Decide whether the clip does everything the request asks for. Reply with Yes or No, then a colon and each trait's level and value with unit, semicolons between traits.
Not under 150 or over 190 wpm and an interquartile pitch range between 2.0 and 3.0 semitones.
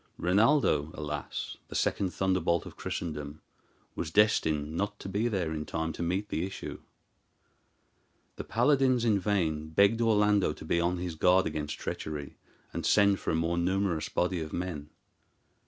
No: average, 155 wpm; average, 4.4 semitones